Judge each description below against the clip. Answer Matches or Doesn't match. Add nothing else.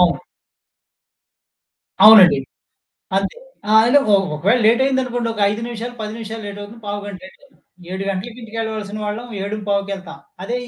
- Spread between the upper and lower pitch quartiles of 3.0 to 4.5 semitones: Doesn't match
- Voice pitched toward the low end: Doesn't match